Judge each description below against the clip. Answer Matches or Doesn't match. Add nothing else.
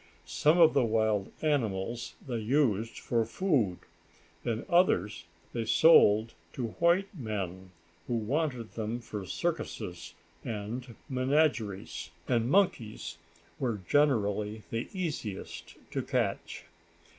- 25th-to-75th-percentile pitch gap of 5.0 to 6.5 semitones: Matches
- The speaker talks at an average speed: Doesn't match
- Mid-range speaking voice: Doesn't match